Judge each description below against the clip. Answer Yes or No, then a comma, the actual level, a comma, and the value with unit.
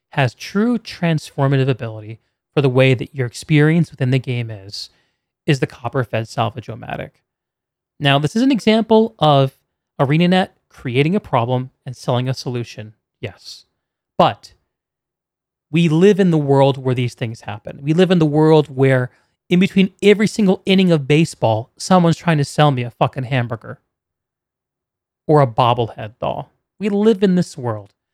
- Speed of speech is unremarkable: Yes, average, 160 wpm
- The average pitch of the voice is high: No, medium, 140 Hz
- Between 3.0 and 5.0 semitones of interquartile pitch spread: No, wide, 5.5 semitones